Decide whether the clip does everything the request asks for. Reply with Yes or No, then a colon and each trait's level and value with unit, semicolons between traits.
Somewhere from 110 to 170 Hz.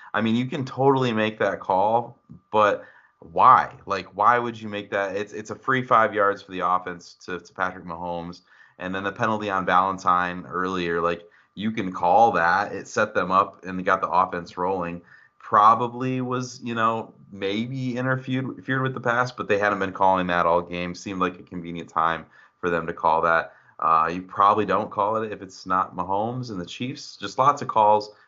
No: low, 100 Hz